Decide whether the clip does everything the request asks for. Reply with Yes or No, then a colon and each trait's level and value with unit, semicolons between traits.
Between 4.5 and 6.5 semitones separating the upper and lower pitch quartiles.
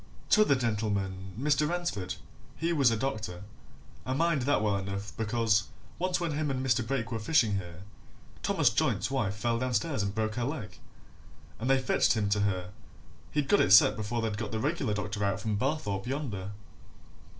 Yes: average, 5.0 semitones